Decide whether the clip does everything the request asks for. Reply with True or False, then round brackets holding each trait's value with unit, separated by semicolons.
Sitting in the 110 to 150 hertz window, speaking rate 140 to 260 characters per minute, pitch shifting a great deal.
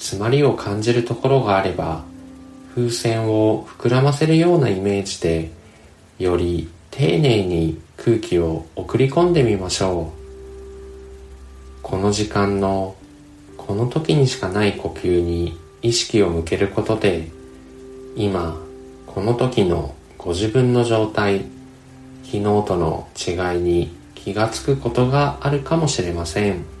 False (100 Hz; 240 characters per minute; 6.2 semitones)